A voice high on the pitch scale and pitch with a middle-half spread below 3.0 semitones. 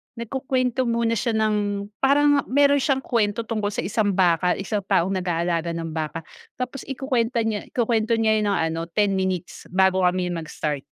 No: high, 210 Hz; average, 4.9 semitones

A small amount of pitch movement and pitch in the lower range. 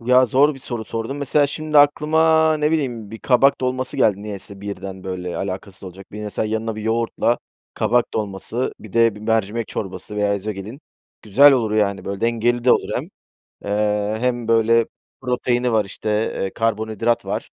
No: average, 3.4 semitones; low, 115 Hz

